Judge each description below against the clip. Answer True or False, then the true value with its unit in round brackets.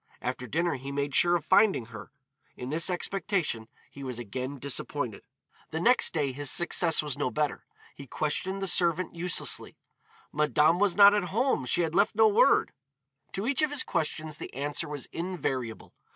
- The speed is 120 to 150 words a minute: False (175 wpm)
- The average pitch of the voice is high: False (155 Hz)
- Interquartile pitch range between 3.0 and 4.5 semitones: False (5.0 semitones)